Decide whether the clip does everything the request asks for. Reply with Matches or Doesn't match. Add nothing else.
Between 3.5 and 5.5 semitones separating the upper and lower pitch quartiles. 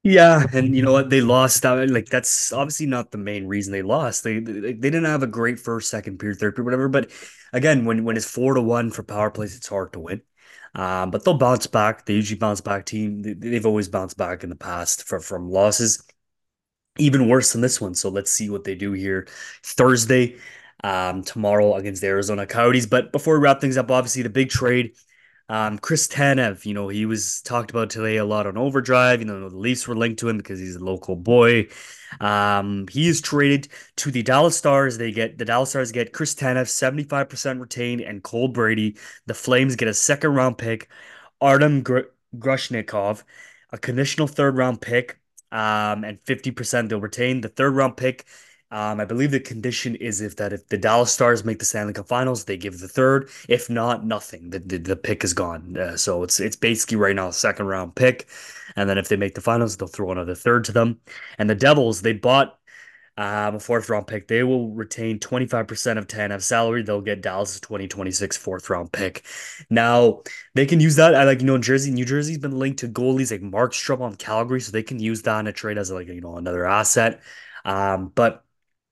Matches